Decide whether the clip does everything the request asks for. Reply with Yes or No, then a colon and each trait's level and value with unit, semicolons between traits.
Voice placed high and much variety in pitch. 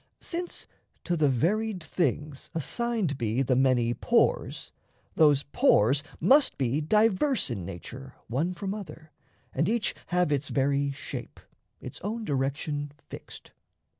No: medium, 150 Hz; wide, 6.9 semitones